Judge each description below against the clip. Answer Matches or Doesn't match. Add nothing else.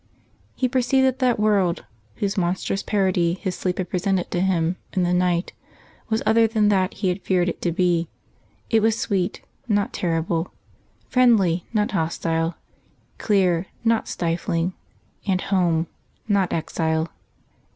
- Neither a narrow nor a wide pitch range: Matches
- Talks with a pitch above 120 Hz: Matches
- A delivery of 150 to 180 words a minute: Doesn't match